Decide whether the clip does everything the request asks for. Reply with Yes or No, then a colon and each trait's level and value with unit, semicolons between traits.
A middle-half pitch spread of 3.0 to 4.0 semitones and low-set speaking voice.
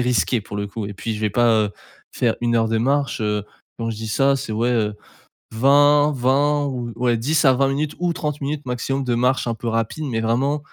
Yes: average, 3.6 semitones; low, 120 Hz